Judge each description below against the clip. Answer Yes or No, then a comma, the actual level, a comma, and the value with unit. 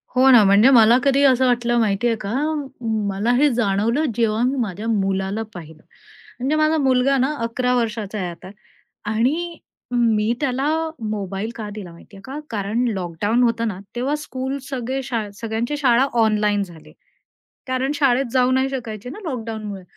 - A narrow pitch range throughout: No, average, 3.8 semitones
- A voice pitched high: Yes, high, 230 Hz